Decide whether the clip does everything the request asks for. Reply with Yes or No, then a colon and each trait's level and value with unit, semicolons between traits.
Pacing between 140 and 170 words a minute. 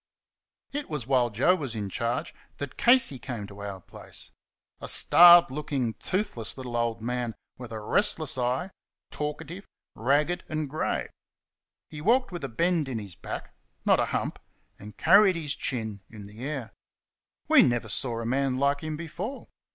Yes: average, 165 wpm